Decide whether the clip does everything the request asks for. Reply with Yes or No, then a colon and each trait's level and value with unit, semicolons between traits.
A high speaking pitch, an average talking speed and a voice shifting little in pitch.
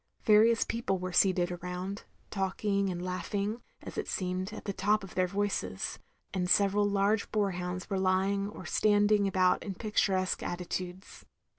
Yes: high, 195 Hz; average, 160 wpm; narrow, 2.0 semitones